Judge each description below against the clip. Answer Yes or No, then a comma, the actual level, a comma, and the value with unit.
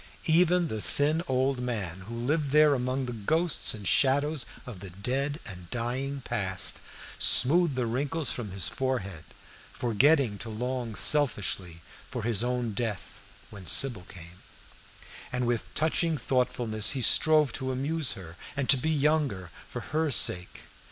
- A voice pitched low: Yes, low, 125 Hz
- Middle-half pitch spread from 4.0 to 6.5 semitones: Yes, average, 5.2 semitones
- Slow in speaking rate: No, average, 150 wpm